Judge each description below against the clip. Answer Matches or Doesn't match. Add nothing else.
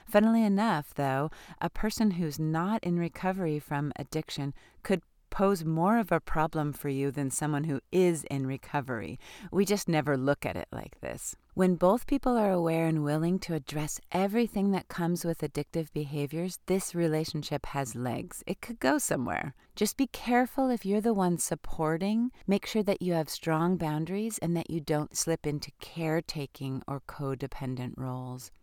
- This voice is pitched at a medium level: Matches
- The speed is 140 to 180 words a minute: Matches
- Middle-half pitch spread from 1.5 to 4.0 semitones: Doesn't match